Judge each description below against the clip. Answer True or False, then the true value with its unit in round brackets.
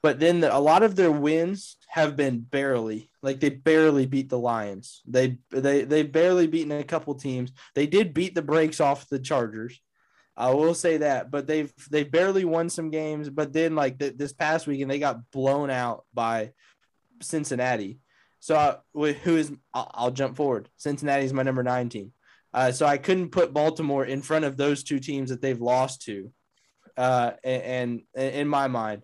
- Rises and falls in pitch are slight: False (3.5 semitones)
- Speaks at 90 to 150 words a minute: False (195 wpm)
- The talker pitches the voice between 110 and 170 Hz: True (140 Hz)